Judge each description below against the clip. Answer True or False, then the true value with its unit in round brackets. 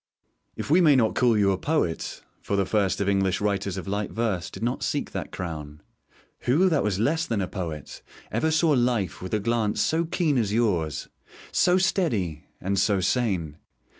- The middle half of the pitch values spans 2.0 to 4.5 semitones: False (5.1 semitones)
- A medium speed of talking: True (190 wpm)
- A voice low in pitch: True (105 Hz)